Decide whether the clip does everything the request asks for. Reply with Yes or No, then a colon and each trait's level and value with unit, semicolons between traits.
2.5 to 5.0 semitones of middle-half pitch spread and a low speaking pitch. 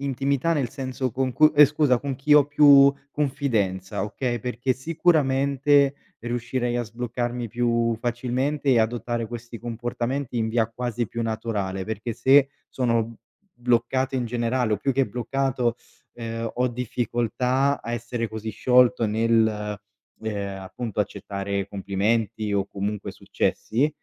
Yes: average, 2.9 semitones; low, 120 Hz